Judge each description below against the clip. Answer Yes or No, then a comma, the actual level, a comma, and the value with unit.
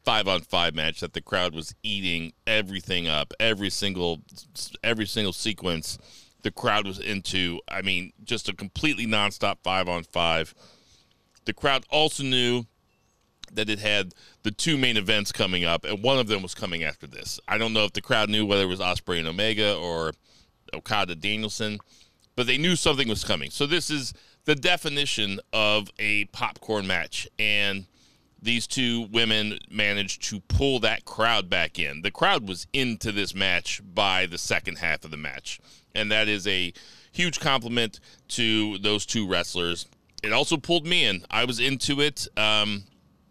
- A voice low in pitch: Yes, low, 105 Hz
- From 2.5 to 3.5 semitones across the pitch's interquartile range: No, average, 4.1 semitones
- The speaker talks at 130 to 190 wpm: Yes, average, 175 wpm